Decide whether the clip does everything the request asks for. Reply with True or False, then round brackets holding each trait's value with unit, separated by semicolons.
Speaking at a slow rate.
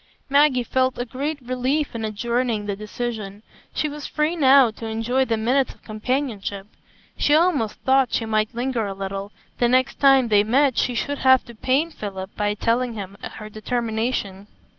False (175 wpm)